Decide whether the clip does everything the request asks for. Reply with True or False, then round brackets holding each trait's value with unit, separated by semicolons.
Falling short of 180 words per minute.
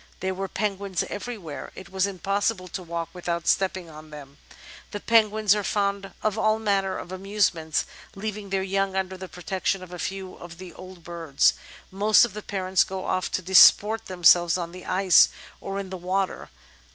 False (185 wpm)